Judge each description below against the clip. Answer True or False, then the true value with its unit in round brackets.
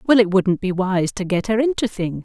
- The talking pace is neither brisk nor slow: False (270 wpm)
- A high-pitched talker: True (200 Hz)